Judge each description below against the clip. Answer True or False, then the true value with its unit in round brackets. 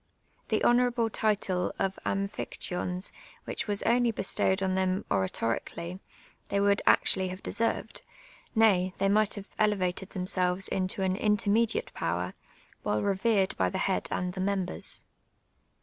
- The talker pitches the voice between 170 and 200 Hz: True (190 Hz)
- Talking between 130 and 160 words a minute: True (140 wpm)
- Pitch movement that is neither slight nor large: False (2.3 semitones)